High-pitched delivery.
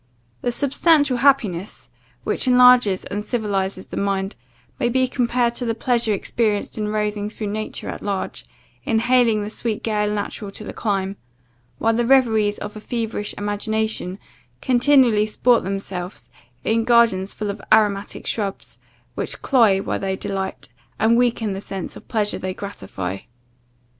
Yes: high, 215 Hz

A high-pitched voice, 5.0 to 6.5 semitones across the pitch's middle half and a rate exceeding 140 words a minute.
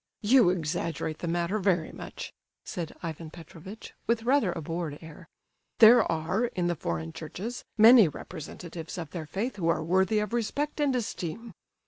No: medium, 175 Hz; average, 5.3 semitones; average, 160 wpm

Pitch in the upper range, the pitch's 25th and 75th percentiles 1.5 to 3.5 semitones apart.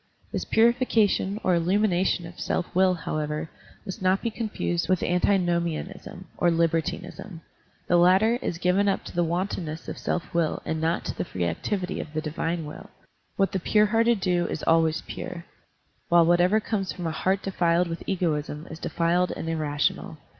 No: medium, 175 Hz; average, 2.7 semitones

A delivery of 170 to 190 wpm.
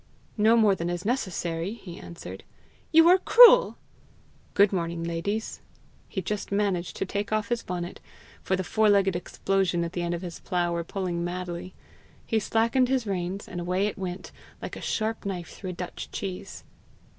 Yes: average, 180 wpm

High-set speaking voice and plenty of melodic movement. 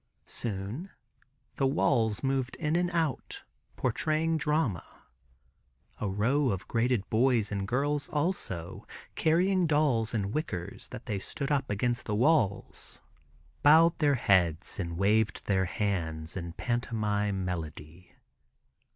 No: low, 115 Hz; wide, 7.0 semitones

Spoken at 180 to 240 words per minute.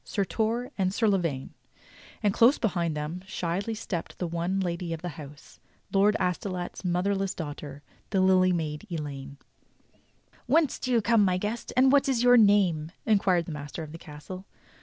Yes: average, 185 wpm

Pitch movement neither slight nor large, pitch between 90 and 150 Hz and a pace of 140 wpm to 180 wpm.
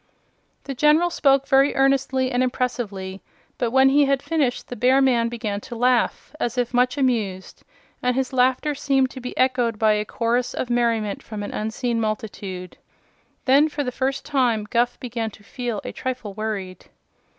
No: average, 3.3 semitones; high, 245 Hz; average, 175 wpm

